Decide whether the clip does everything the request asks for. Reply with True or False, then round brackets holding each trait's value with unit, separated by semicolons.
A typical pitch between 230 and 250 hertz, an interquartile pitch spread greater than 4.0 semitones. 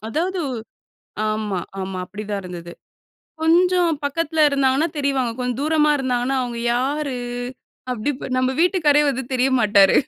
False (265 Hz; 4.6 semitones)